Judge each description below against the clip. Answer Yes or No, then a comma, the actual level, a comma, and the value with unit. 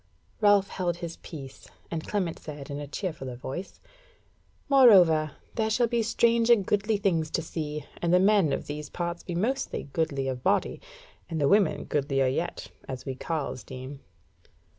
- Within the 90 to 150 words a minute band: No, average, 165 wpm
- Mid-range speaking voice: Yes, medium, 165 Hz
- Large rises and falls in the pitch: Yes, wide, 5.9 semitones